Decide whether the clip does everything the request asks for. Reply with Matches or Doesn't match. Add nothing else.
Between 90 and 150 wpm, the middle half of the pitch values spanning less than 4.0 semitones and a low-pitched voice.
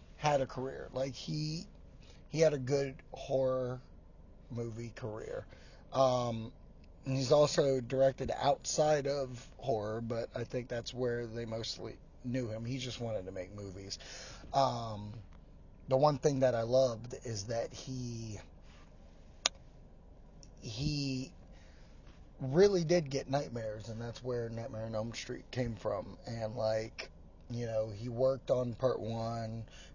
Matches